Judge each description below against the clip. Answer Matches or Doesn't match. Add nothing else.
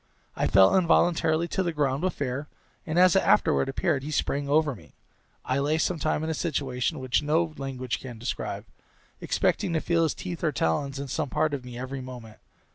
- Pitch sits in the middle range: Matches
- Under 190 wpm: Doesn't match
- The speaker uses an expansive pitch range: Doesn't match